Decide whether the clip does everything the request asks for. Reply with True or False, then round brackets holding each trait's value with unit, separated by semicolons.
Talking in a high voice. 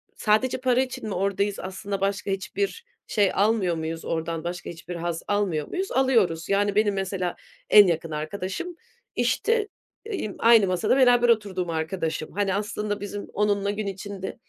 True (200 Hz)